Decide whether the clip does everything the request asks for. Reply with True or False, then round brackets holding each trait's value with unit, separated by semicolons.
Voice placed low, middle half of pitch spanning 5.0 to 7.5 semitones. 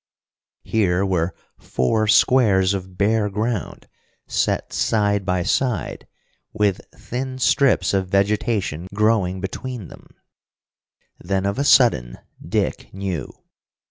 False (100 Hz; 3.2 semitones)